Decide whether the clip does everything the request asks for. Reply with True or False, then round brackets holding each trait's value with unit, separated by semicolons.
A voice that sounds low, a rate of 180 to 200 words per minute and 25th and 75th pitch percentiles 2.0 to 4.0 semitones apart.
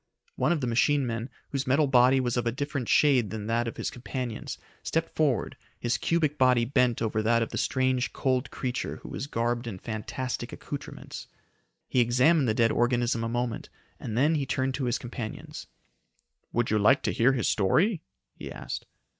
True (125 Hz; 190 wpm; 2.5 semitones)